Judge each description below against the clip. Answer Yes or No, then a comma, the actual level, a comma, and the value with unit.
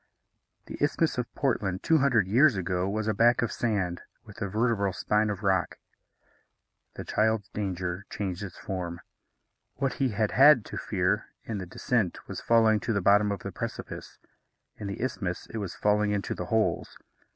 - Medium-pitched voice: No, low, 105 Hz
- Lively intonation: No, average, 3.2 semitones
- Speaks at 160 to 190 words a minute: Yes, average, 175 wpm